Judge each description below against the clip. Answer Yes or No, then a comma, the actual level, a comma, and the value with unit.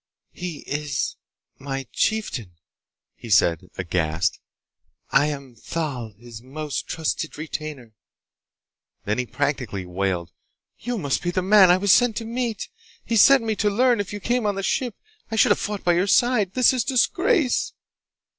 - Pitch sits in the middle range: Yes, medium, 165 Hz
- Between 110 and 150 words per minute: No, average, 160 wpm